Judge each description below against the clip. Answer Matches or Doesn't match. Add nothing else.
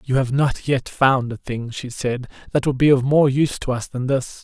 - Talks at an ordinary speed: Doesn't match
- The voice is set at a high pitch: Doesn't match